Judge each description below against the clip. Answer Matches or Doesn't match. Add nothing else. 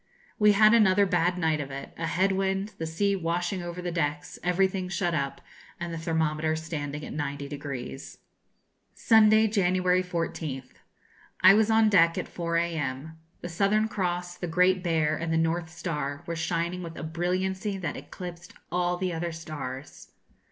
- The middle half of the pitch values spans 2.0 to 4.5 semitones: Matches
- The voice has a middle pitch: Matches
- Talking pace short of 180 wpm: Matches